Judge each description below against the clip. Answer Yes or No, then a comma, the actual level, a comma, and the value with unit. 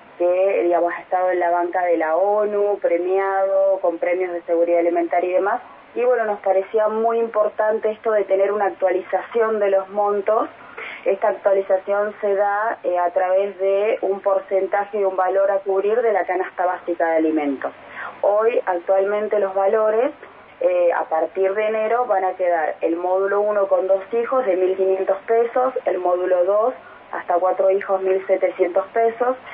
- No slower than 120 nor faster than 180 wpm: Yes, average, 165 wpm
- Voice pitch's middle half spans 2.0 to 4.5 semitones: Yes, narrow, 2.5 semitones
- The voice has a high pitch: Yes, high, 195 Hz